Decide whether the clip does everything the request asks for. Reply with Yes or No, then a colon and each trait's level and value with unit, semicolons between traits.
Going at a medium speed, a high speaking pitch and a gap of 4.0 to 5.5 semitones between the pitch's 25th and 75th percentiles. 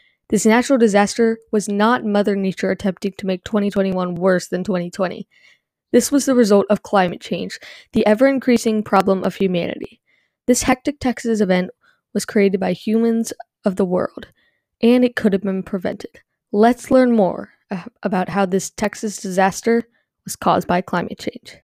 No: average, 160 wpm; high, 210 Hz; average, 3.2 semitones